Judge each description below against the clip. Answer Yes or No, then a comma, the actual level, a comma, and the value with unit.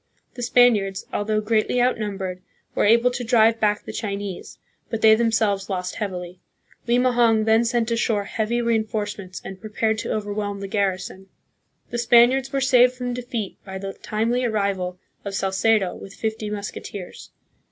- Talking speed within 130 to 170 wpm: Yes, average, 155 wpm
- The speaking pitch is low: No, high, 215 Hz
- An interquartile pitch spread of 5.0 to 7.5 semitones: No, average, 3.0 semitones